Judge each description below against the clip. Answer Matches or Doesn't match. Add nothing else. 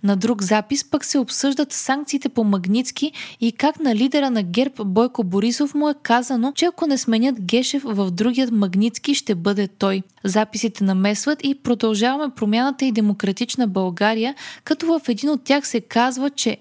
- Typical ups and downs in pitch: Matches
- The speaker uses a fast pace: Matches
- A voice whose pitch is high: Matches